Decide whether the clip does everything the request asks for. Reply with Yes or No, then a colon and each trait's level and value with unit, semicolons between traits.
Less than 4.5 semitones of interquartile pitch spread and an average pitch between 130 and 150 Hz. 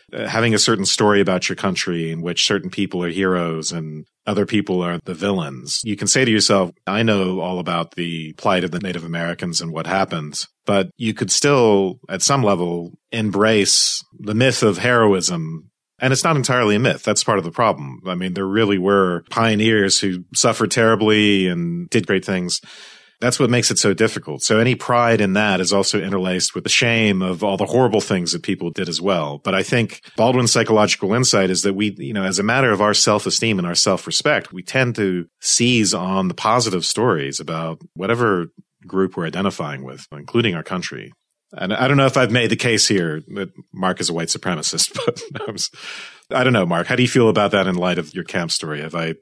No: average, 4.0 semitones; low, 100 Hz